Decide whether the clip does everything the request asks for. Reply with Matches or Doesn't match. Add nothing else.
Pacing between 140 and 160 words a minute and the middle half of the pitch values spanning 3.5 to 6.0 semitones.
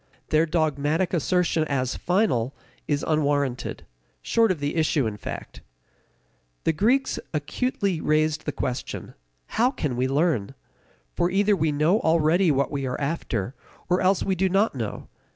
Matches